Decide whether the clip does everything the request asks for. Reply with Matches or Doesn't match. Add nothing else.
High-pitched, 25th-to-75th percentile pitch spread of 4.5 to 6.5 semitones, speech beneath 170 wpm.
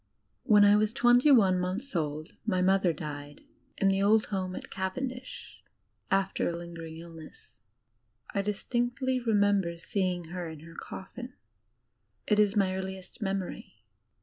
Doesn't match